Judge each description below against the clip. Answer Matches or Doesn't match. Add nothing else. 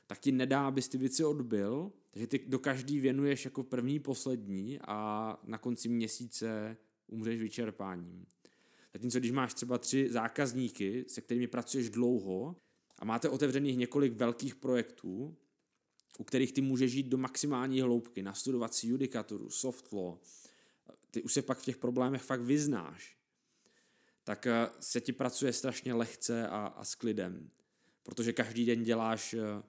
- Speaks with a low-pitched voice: Matches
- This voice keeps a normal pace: Matches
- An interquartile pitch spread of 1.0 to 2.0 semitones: Doesn't match